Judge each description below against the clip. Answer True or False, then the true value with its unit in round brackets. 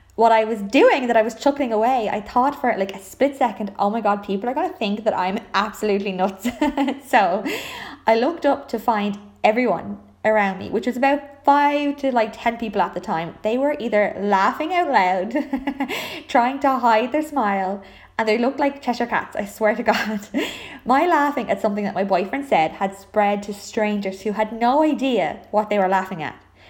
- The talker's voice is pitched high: True (225 Hz)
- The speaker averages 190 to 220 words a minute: True (200 wpm)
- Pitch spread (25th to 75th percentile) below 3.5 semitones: False (5.1 semitones)